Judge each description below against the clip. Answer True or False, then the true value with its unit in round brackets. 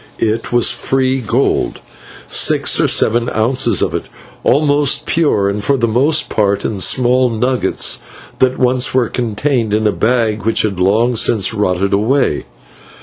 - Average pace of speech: True (150 wpm)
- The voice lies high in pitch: False (120 Hz)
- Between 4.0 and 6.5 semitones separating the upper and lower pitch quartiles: False (3.3 semitones)